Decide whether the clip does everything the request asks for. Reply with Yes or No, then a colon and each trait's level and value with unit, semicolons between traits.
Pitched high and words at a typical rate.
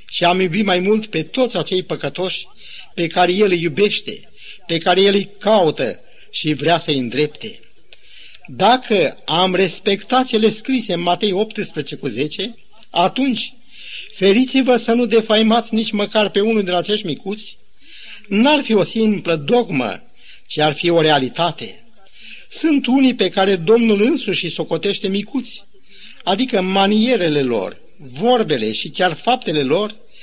Yes: high, 200 Hz; average, 145 wpm